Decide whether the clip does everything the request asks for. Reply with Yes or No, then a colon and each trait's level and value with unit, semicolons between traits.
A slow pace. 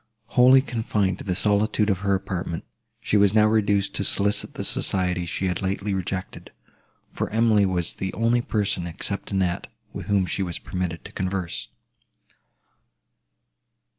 No: average, 150 wpm